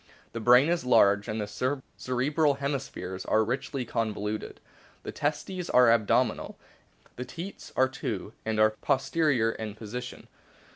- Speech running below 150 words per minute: Yes, average, 140 wpm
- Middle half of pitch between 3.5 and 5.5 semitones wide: Yes, average, 4.4 semitones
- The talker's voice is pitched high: No, low, 125 Hz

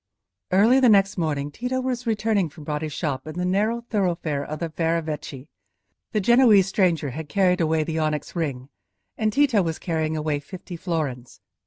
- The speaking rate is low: No, average, 170 wpm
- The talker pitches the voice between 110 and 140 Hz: No, medium, 170 Hz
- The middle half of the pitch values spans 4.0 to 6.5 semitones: Yes, average, 5.1 semitones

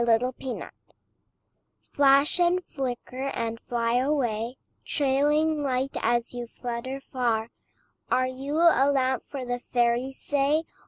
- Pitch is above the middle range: Yes, very high, 260 Hz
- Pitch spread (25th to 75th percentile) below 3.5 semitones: Yes, average, 2.8 semitones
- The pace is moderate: No, slow, 120 wpm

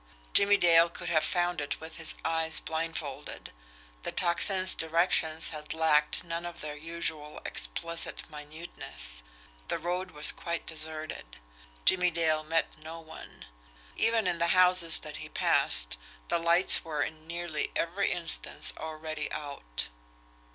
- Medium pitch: Yes, medium, 160 Hz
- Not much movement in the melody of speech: Yes, narrow, 2.0 semitones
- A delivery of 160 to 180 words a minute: No, slow, 135 wpm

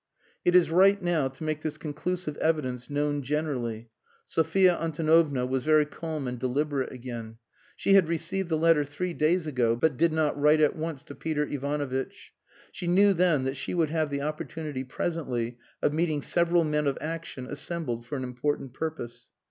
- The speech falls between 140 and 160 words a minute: No, average, 175 wpm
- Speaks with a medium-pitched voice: Yes, medium, 150 Hz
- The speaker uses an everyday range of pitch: Yes, average, 3.7 semitones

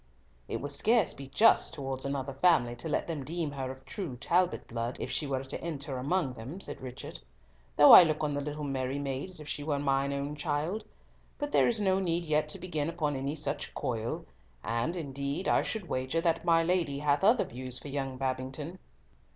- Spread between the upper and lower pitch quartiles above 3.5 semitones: Yes, average, 4.0 semitones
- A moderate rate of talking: No, fast, 210 wpm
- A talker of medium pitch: Yes, medium, 145 Hz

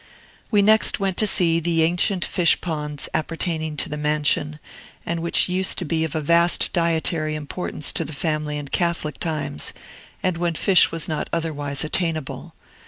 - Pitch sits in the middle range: Yes, medium, 165 Hz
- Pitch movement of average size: No, narrow, 2.2 semitones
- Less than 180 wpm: Yes, average, 165 wpm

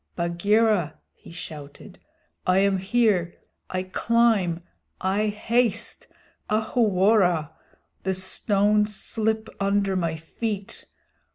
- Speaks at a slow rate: Yes, slow, 90 wpm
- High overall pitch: Yes, high, 200 Hz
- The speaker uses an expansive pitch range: No, average, 3.2 semitones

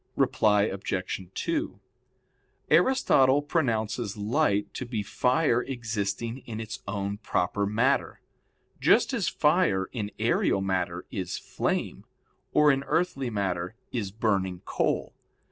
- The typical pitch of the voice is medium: No, low, 110 Hz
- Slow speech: Yes, slow, 115 wpm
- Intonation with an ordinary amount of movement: Yes, average, 4.8 semitones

